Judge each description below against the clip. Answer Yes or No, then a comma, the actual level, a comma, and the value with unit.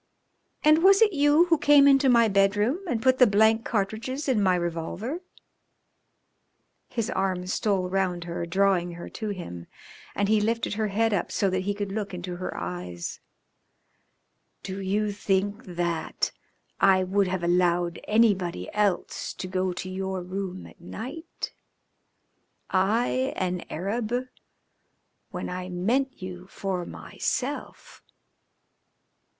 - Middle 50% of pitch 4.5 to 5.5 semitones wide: No, average, 3.9 semitones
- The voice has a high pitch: Yes, high, 195 Hz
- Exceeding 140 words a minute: No, slow, 135 wpm